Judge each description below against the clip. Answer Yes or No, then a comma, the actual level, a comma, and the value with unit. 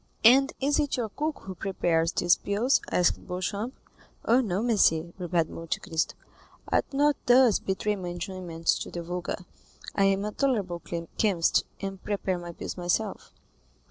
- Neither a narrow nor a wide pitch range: Yes, average, 4.7 semitones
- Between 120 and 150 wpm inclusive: No, average, 160 wpm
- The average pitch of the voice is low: No, high, 195 Hz